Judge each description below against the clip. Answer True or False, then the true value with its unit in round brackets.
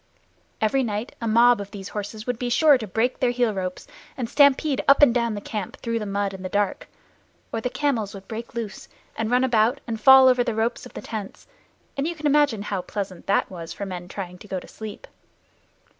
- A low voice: False (225 Hz)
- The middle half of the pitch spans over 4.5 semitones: False (3.6 semitones)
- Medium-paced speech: False (225 wpm)